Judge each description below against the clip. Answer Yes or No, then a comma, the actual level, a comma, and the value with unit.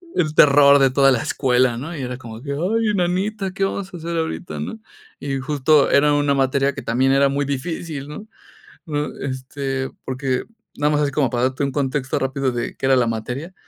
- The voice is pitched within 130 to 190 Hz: Yes, medium, 140 Hz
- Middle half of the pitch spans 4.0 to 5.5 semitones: No, average, 2.7 semitones